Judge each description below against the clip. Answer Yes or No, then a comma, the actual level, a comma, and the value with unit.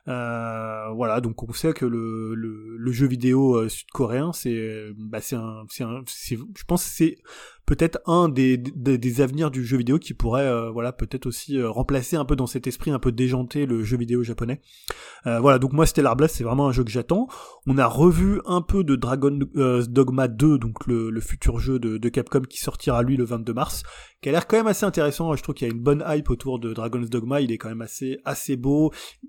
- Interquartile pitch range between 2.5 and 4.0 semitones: Yes, average, 3.5 semitones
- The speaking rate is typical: No, fast, 230 wpm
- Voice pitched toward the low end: Yes, low, 130 Hz